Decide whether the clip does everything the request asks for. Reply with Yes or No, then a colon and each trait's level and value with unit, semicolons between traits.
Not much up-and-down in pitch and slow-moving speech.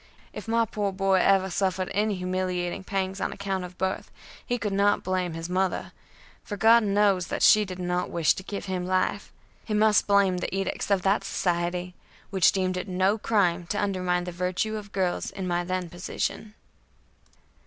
No: narrow, 1.9 semitones; average, 185 wpm